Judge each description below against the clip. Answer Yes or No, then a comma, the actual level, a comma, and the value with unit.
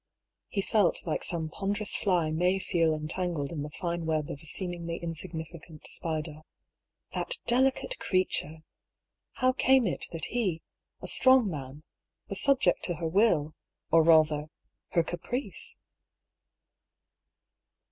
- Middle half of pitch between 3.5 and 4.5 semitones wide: Yes, average, 3.9 semitones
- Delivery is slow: Yes, slow, 130 wpm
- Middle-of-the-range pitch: Yes, medium, 170 Hz